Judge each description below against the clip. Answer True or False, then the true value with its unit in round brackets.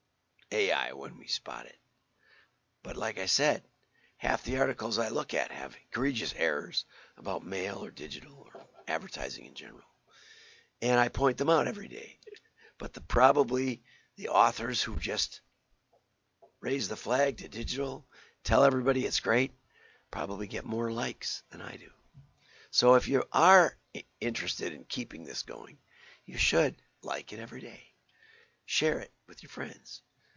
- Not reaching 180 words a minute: True (150 wpm)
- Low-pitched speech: True (130 Hz)